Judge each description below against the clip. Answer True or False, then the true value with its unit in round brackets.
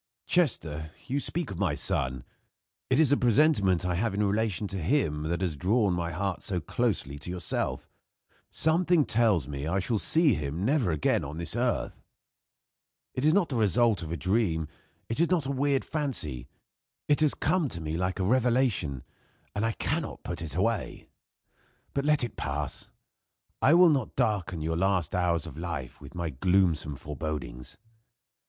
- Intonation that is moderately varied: False (8.2 semitones)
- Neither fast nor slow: True (170 wpm)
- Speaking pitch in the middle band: False (95 Hz)